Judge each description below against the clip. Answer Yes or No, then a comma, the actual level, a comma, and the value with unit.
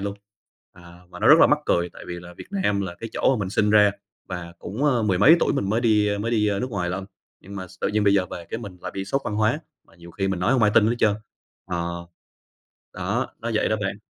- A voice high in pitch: No, low, 100 Hz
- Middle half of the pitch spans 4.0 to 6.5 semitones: No, average, 3.2 semitones